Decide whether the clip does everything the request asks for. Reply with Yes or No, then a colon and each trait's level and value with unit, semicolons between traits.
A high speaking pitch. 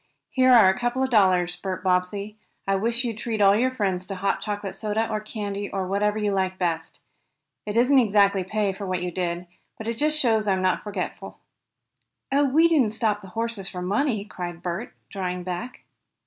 Yes: high, 205 Hz